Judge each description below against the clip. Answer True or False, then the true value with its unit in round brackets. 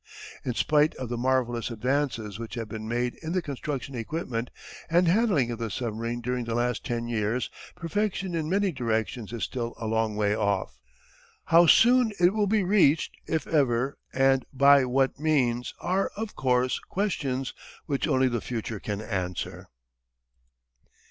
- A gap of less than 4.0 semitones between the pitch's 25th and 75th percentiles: False (5.3 semitones)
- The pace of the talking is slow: False (160 wpm)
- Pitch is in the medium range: False (125 Hz)